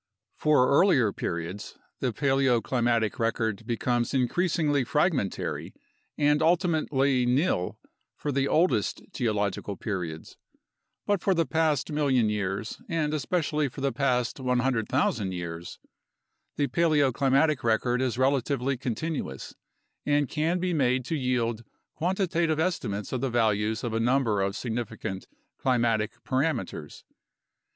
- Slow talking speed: Yes, slow, 115 wpm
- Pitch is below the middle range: Yes, low, 130 Hz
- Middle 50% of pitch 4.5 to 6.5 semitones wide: Yes, average, 4.8 semitones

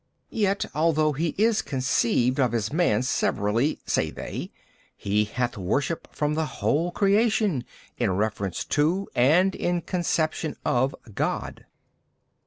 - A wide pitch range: Yes, wide, 6.3 semitones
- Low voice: No, medium, 150 Hz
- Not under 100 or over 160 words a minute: Yes, slow, 135 wpm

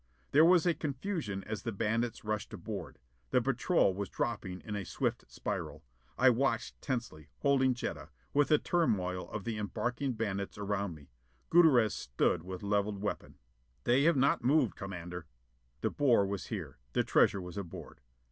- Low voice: Yes, low, 110 Hz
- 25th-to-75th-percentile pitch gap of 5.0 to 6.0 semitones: Yes, wide, 5.6 semitones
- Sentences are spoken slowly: No, average, 160 wpm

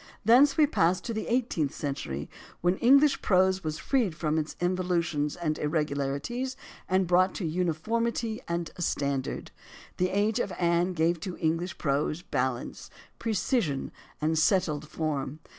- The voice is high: No, medium, 175 Hz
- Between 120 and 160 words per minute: Yes, average, 155 wpm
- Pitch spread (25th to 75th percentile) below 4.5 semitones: No, average, 4.9 semitones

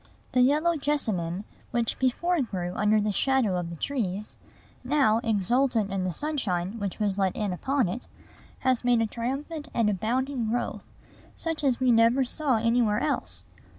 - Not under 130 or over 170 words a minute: Yes, average, 160 wpm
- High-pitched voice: Yes, high, 235 Hz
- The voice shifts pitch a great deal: No, average, 4.6 semitones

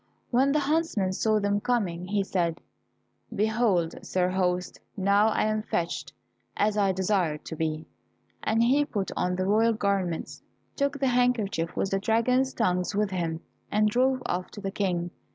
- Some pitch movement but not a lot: Yes, average, 4.1 semitones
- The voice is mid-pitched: No, high, 200 Hz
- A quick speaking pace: No, average, 165 wpm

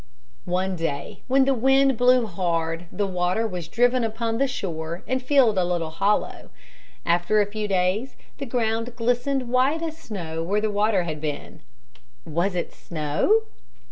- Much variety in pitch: Yes, wide, 6.0 semitones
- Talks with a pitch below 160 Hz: No, high, 210 Hz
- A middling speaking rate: Yes, average, 160 wpm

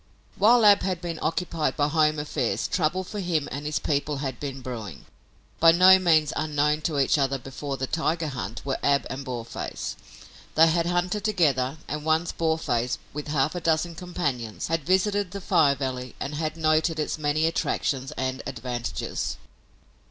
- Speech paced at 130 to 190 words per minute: Yes, average, 170 wpm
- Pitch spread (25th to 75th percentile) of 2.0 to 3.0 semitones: No, average, 3.8 semitones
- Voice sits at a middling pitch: Yes, medium, 150 Hz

